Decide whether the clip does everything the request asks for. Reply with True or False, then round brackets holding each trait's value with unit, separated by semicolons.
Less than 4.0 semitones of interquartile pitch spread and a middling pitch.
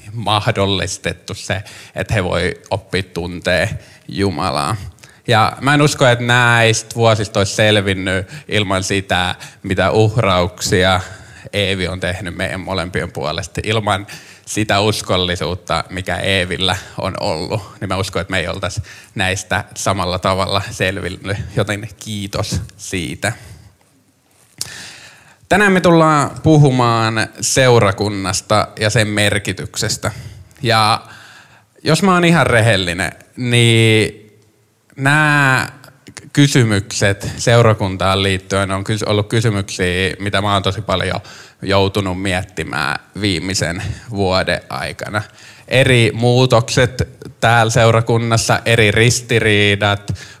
False (3.2 semitones; 105 Hz)